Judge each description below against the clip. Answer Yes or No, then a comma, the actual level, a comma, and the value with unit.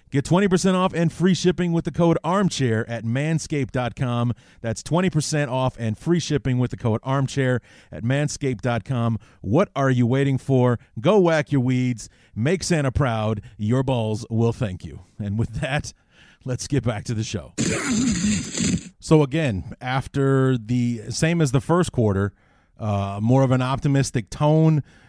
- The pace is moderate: Yes, average, 155 wpm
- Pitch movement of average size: Yes, average, 4.6 semitones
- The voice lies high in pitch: No, low, 130 Hz